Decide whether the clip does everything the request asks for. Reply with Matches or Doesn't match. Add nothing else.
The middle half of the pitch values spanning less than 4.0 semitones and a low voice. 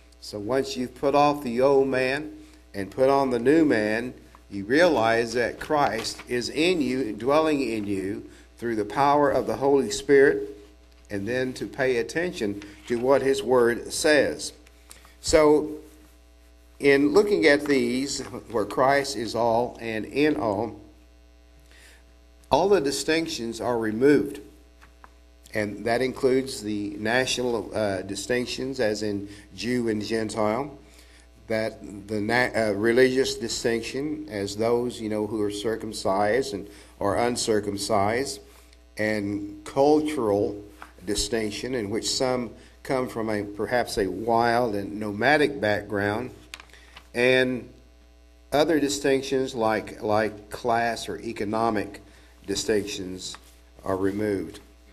Doesn't match